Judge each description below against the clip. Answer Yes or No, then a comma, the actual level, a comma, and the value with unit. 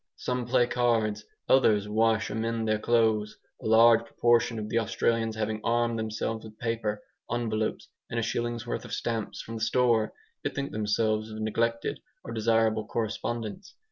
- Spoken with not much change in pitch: Yes, narrow, 1.3 semitones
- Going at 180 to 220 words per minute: No, average, 160 wpm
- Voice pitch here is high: No, low, 115 Hz